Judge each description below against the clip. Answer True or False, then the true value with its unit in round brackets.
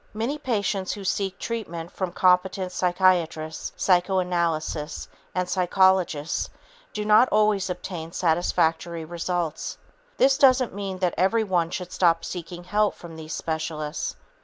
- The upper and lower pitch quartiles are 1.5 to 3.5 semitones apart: True (2.8 semitones)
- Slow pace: True (120 wpm)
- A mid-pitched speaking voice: True (180 Hz)